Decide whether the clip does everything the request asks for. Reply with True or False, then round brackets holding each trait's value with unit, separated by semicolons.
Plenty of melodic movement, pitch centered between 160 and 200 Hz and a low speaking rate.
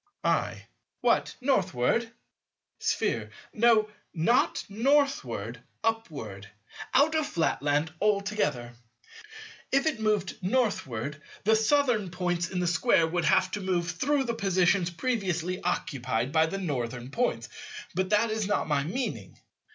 True (6.0 semitones; 185 Hz; 125 wpm)